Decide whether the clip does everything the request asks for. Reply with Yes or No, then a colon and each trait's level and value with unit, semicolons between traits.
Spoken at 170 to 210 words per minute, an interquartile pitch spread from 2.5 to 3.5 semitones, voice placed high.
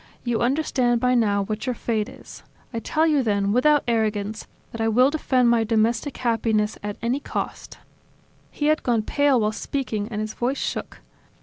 Yes: average, 180 wpm; average, 3.2 semitones; high, 235 Hz